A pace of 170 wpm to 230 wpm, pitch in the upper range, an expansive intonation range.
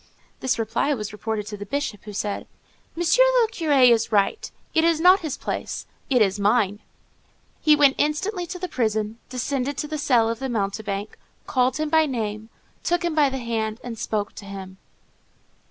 Yes: average, 185 wpm; very high, 250 Hz; wide, 6.2 semitones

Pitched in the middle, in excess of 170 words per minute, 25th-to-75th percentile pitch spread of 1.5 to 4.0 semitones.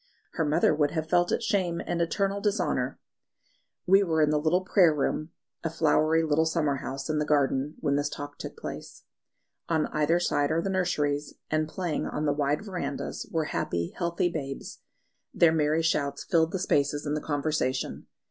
Yes: medium, 155 Hz; average, 180 wpm; average, 2.7 semitones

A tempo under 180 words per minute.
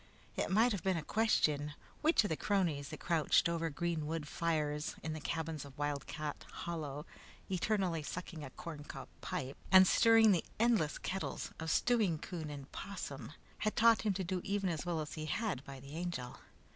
No: average, 185 wpm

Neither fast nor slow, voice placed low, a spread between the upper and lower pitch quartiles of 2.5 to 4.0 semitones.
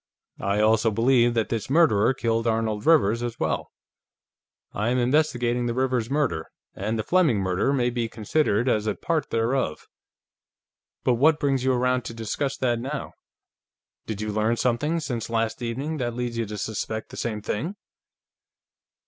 Yes: average, 165 wpm; low, 120 Hz; average, 3.1 semitones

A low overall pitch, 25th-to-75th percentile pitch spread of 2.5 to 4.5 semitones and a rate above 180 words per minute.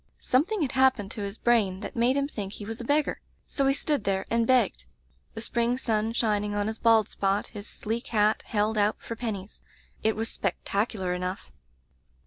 No: high, 220 Hz; average, 2.8 semitones; average, 190 wpm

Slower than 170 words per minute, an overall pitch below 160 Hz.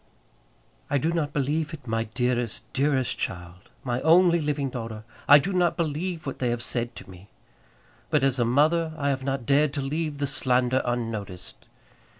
No: average, 175 wpm; low, 135 Hz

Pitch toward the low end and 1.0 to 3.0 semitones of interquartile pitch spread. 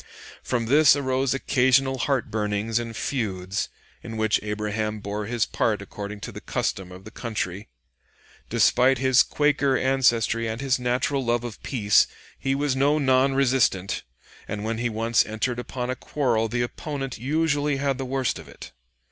No: low, 120 Hz; average, 3.7 semitones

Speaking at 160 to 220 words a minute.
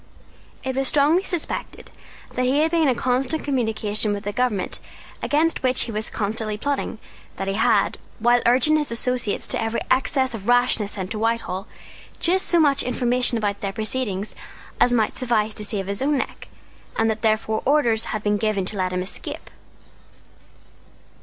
Yes: average, 170 wpm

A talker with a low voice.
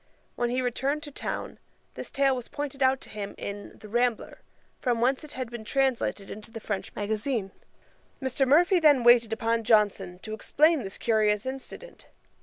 No: high, 240 Hz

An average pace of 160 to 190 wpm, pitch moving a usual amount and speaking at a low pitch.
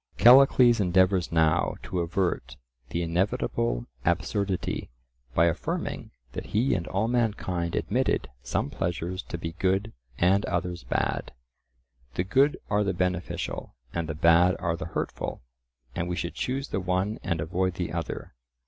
No: average, 145 wpm; average, 3.1 semitones; very low, 90 Hz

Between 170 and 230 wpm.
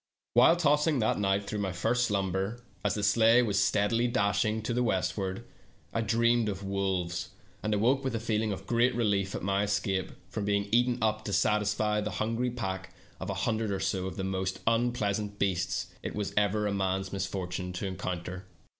Yes: average, 200 wpm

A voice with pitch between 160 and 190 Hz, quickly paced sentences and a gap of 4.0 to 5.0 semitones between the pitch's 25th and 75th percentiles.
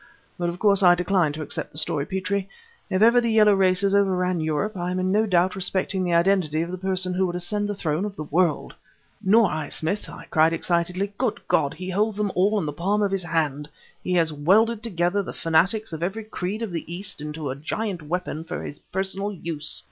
No: medium, 185 Hz; fast, 225 wpm; average, 3.3 semitones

